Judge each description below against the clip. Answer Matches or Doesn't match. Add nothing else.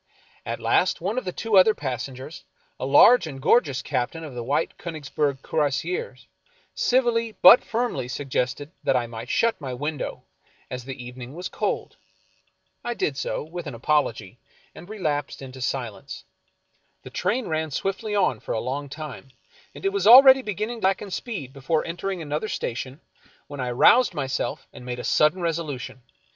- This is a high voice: Doesn't match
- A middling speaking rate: Matches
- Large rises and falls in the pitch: Matches